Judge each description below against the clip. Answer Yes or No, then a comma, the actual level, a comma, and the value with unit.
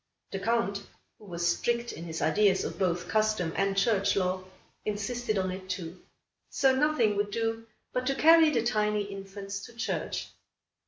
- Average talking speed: Yes, average, 165 wpm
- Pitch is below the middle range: No, high, 205 Hz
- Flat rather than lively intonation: No, average, 3.5 semitones